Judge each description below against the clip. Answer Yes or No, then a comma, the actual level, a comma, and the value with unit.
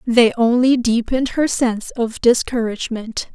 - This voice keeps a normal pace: No, slow, 125 wpm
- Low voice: No, high, 235 Hz